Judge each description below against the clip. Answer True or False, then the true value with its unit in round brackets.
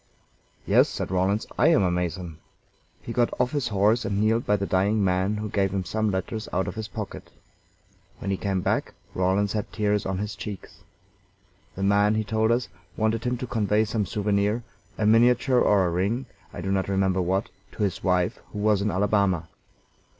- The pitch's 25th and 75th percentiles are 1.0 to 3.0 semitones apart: True (2.4 semitones)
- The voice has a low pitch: True (100 Hz)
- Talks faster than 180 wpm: True (195 wpm)